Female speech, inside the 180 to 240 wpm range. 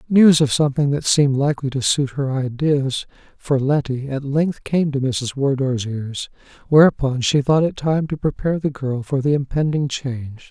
No: male; average, 185 wpm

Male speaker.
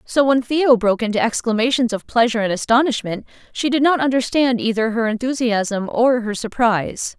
No: female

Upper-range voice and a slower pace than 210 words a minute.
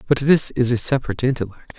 No: low, 125 Hz; average, 200 wpm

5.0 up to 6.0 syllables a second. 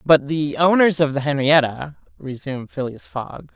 No: 4.6 syllables/s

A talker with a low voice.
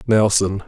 Yes: low, 105 Hz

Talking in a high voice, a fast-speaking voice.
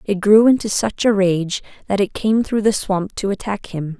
Yes: high, 200 Hz; fast, 225 wpm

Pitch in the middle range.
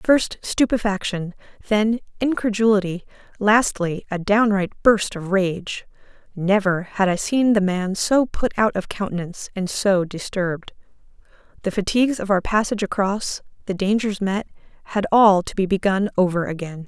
No: high, 200 Hz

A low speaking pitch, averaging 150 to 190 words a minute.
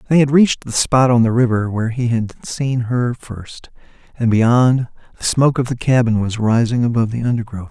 No: low, 120 Hz; average, 200 wpm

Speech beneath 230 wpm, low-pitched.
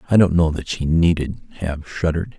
Yes: average, 200 wpm; very low, 85 Hz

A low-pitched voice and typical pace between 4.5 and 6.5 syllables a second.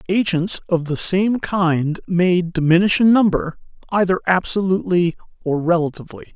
No: medium, 175 Hz; 4.9 syllables/s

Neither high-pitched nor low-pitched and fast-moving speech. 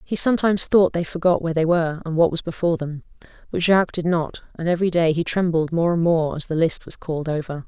Yes: medium, 170 Hz; fast, 240 wpm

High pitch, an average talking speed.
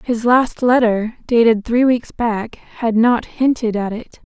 Yes: high, 235 Hz; average, 165 wpm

